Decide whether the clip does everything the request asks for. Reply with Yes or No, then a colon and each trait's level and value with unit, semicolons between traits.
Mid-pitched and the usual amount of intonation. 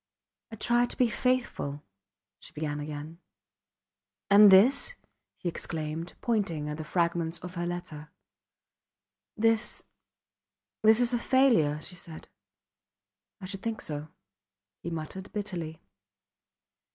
No: medium, 175 Hz; wide, 5.9 semitones